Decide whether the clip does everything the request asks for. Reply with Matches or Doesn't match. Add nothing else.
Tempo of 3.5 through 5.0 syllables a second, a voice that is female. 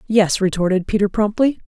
Doesn't match